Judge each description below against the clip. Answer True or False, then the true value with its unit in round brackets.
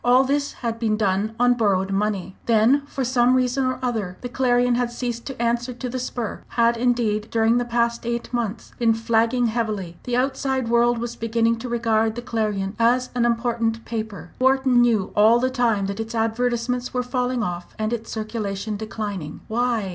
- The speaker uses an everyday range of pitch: False (2.0 semitones)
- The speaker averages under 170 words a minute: False (185 wpm)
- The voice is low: False (235 Hz)